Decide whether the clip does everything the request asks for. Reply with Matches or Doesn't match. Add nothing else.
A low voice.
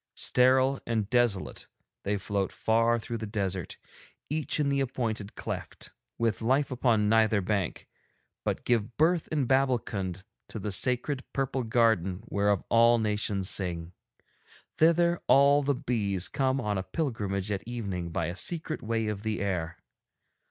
Matches